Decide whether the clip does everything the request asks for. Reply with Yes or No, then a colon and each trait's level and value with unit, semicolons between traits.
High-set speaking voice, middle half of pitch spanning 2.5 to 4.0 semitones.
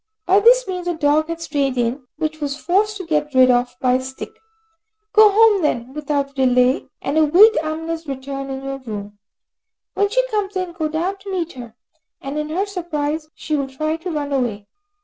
No: very high, 305 Hz; average, 5.0 semitones